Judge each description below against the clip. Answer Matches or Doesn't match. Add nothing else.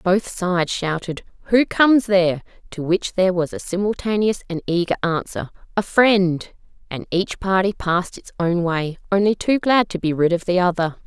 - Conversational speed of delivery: Matches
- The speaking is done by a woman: Matches